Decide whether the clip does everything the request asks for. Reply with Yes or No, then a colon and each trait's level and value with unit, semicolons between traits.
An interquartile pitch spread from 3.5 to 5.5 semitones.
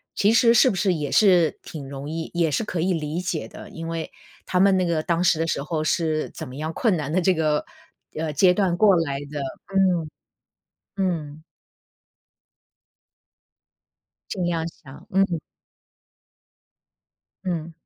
No: average, 3.0 semitones